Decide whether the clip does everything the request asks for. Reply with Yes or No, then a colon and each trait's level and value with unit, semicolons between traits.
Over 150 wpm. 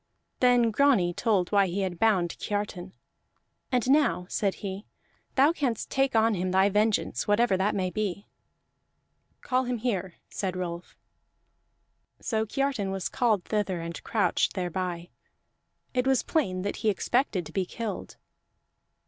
No: average, 140 wpm